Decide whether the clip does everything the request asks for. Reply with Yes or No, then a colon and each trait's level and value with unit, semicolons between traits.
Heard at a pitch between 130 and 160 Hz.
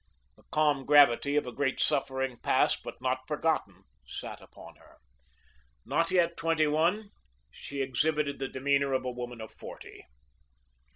Yes: medium, 140 Hz